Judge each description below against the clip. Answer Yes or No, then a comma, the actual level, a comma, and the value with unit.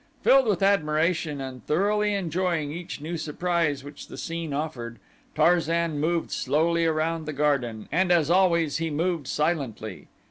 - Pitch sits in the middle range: Yes, medium, 160 Hz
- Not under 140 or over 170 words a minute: Yes, average, 145 wpm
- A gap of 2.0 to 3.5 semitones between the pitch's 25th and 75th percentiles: Yes, average, 2.8 semitones